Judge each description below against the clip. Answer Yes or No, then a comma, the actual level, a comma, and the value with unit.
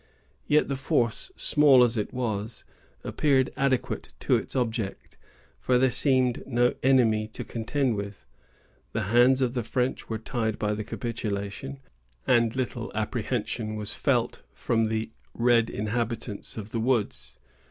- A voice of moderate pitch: No, low, 115 Hz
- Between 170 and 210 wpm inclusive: No, average, 140 wpm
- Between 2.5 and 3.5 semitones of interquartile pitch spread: Yes, average, 2.9 semitones